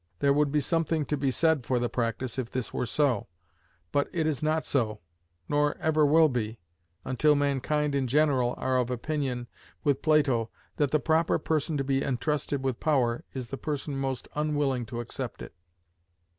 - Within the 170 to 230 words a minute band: Yes, average, 180 wpm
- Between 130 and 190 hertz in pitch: Yes, medium, 140 Hz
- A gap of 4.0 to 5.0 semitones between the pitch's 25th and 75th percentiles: No, average, 3.2 semitones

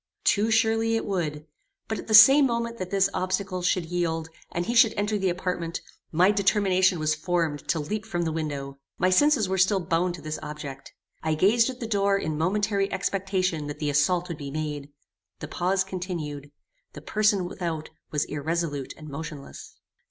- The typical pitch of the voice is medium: Yes, medium, 180 Hz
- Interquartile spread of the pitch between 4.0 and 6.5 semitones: Yes, average, 4.4 semitones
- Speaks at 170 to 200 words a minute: Yes, average, 180 wpm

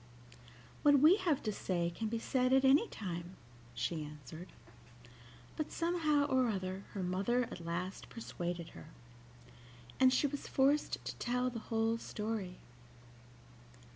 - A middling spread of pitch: No, wide, 6.7 semitones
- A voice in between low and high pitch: No, high, 225 Hz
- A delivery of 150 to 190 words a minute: No, average, 140 wpm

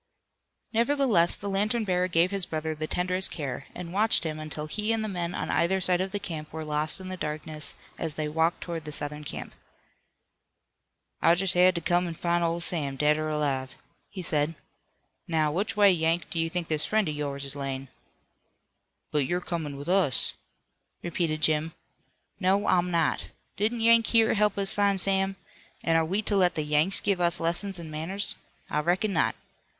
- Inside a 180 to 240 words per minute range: Yes, average, 190 wpm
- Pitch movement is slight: No, average, 3.9 semitones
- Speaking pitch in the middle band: Yes, medium, 170 Hz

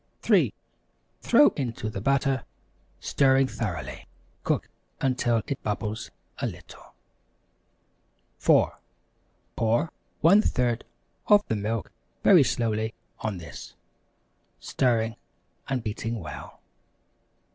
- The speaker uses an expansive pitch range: No, average, 3.5 semitones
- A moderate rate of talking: No, slow, 90 wpm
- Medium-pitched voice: No, low, 115 Hz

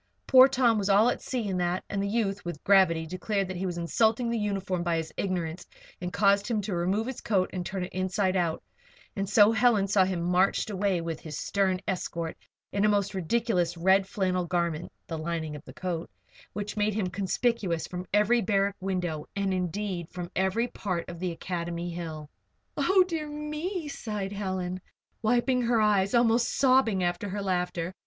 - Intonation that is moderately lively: Yes, average, 3.2 semitones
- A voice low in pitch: No, high, 190 Hz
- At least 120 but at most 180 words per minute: No, average, 195 wpm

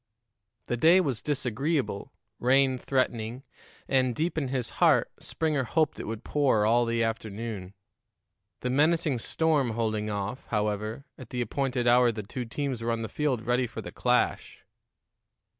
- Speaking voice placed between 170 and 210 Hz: No, low, 125 Hz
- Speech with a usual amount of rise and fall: Yes, average, 3.6 semitones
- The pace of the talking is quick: No, average, 155 wpm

